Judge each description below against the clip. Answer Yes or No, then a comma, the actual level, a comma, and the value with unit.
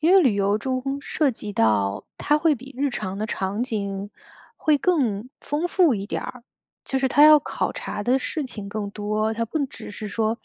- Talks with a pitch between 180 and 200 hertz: No, high, 230 Hz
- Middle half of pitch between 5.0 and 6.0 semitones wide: Yes, wide, 5.6 semitones